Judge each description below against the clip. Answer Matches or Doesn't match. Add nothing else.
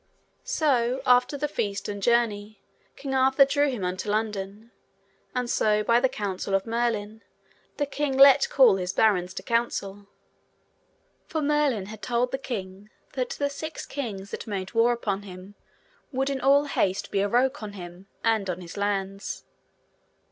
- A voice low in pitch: Doesn't match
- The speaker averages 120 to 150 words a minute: Doesn't match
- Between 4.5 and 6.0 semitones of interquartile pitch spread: Matches